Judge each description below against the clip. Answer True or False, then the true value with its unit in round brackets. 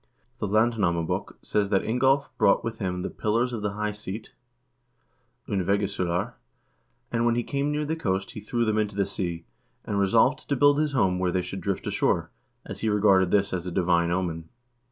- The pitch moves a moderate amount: True (4.1 semitones)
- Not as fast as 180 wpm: False (190 wpm)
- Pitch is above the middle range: False (105 Hz)